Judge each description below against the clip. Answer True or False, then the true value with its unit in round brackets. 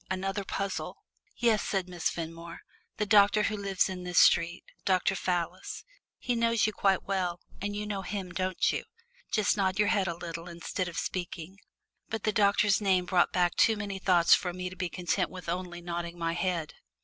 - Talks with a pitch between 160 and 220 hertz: True (185 Hz)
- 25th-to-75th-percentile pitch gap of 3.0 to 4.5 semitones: False (2.6 semitones)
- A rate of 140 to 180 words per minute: False (190 wpm)